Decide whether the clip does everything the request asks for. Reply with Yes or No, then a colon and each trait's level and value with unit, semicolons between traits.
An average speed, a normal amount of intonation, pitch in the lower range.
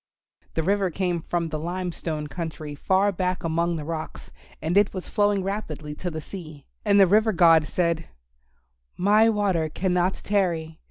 No: average, 165 wpm; average, 3.5 semitones; medium, 175 Hz